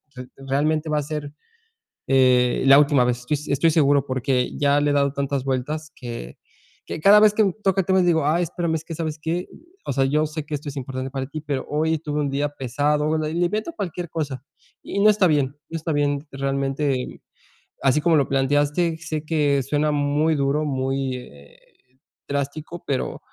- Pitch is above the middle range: No, medium, 145 Hz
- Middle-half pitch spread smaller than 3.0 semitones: Yes, narrow, 2.6 semitones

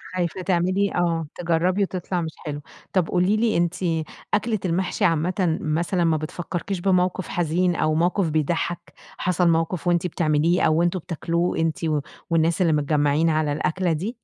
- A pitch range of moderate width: No, narrow, 2.3 semitones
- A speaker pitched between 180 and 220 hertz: No, medium, 170 Hz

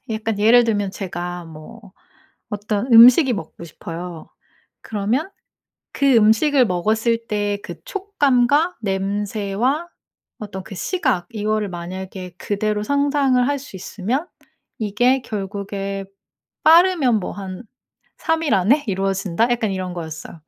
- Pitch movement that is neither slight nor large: Yes, average, 4.7 semitones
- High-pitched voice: Yes, high, 210 Hz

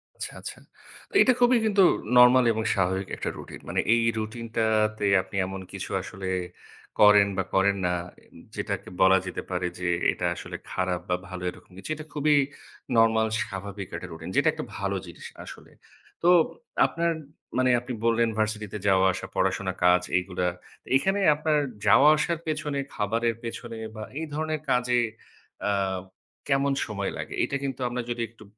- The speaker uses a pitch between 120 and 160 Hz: No, low, 110 Hz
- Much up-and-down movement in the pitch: Yes, wide, 6.0 semitones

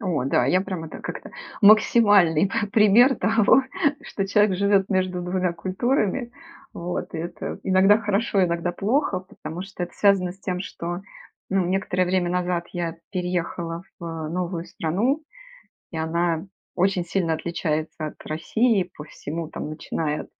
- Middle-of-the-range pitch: Yes, medium, 180 Hz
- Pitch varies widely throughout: No, average, 2.7 semitones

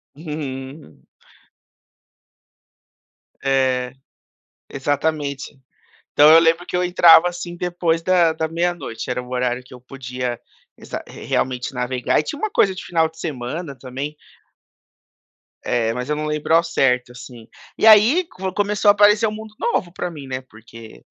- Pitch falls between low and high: Yes, medium, 150 Hz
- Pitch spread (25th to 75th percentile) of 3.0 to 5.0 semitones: No, wide, 5.6 semitones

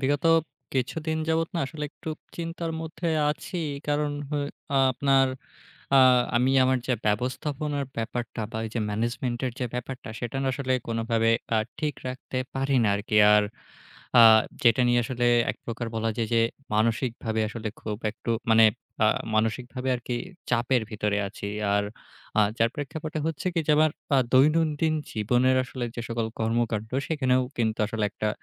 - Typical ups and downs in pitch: Yes, average, 4.1 semitones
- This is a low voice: Yes, low, 125 Hz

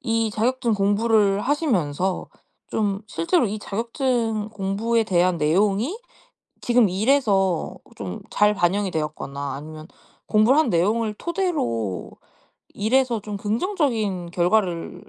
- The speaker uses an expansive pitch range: No, average, 4.4 semitones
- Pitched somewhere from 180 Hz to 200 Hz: No, high, 210 Hz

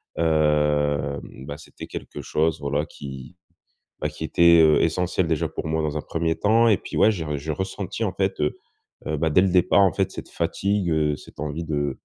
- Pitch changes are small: No, average, 3.4 semitones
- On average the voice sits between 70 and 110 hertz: Yes, very low, 80 Hz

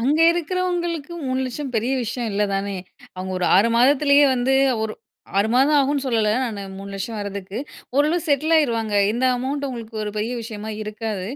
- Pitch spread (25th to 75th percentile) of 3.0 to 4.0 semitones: No, average, 5.2 semitones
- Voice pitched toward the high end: Yes, high, 245 Hz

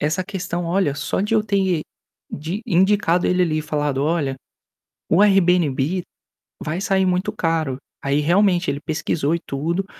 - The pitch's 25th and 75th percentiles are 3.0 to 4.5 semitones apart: Yes, average, 3.9 semitones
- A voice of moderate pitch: Yes, medium, 170 Hz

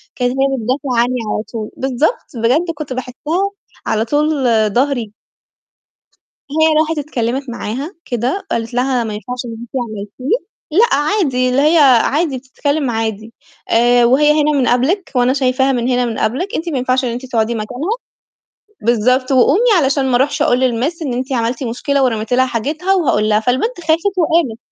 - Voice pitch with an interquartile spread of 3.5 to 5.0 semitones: Yes, average, 3.8 semitones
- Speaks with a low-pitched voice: No, very high, 255 Hz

